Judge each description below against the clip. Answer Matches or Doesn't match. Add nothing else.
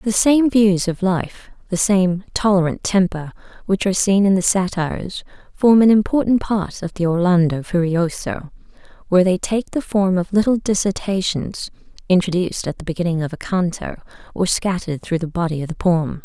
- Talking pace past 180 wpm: Doesn't match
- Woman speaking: Matches